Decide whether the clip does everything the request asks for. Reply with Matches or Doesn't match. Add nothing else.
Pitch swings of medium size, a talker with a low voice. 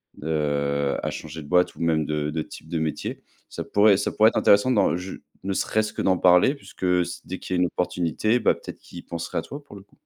Matches